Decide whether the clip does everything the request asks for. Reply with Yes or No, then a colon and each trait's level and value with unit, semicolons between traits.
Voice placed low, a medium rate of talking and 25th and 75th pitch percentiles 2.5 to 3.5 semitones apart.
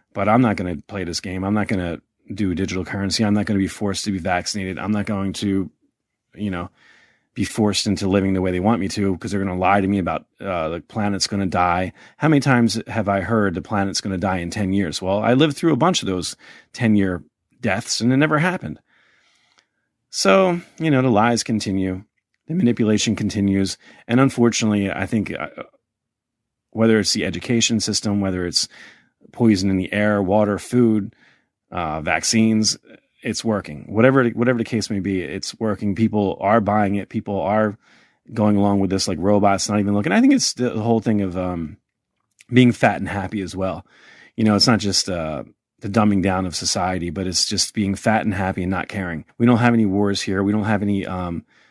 No: low, 100 Hz; fast, 210 wpm; average, 2.9 semitones